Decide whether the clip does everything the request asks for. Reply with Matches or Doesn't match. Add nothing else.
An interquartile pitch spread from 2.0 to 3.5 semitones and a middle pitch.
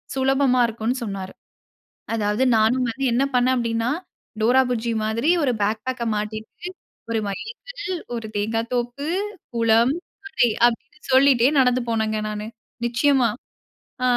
Doesn't match